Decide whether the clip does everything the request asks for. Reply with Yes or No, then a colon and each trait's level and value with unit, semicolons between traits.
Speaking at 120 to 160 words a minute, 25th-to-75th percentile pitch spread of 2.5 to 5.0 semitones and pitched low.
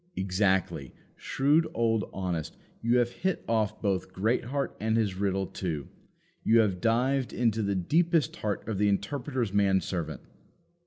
Yes: average, 145 wpm; average, 4.2 semitones; low, 105 Hz